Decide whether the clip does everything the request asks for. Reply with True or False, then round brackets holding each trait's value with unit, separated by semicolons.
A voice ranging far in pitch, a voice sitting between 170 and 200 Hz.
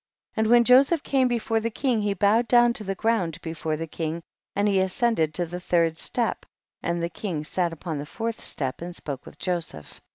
True (5.7 semitones; 190 Hz)